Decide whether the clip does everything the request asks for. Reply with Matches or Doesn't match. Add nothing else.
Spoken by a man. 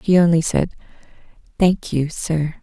Doesn't match